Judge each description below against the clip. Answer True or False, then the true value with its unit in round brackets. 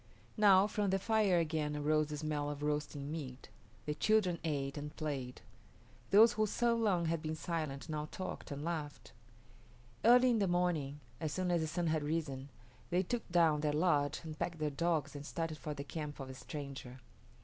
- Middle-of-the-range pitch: True (155 Hz)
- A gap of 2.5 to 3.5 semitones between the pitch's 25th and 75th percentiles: True (3.2 semitones)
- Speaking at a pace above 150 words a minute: True (190 wpm)